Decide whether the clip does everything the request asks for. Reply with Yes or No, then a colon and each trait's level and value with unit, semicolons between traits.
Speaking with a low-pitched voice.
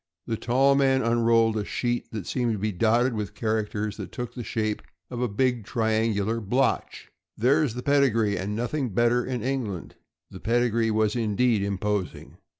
Yes: low, 115 Hz